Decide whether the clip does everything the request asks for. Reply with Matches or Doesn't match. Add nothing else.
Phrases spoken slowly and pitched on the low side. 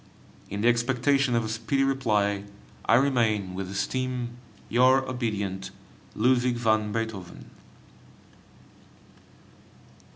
Matches